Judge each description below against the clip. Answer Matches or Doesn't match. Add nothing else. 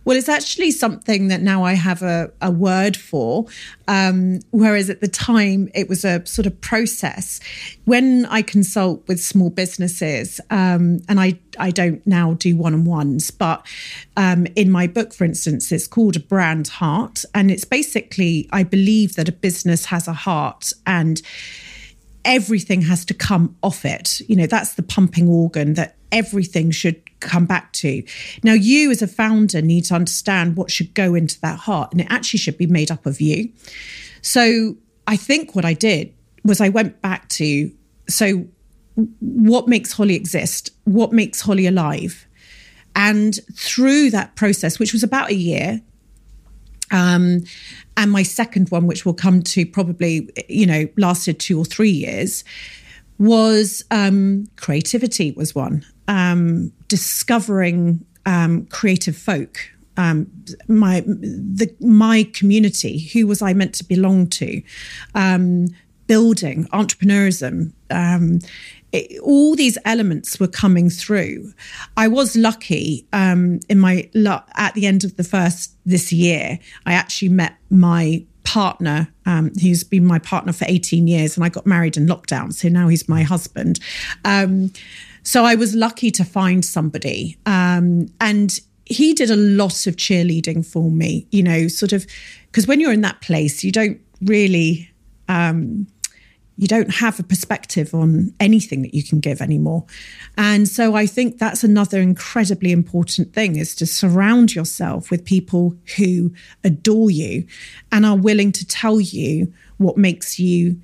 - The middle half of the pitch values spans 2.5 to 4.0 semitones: Matches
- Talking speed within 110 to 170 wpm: Matches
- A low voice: Doesn't match